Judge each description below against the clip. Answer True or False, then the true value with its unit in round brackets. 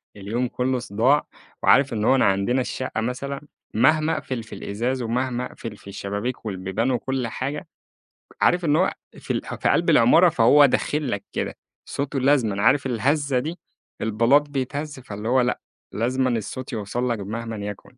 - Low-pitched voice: True (125 Hz)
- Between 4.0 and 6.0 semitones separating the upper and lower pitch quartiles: False (3.6 semitones)